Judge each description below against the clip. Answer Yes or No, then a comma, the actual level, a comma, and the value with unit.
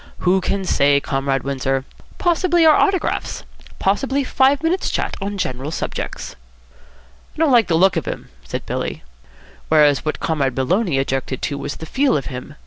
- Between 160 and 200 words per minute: Yes, average, 165 wpm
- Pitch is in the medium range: Yes, medium, 160 Hz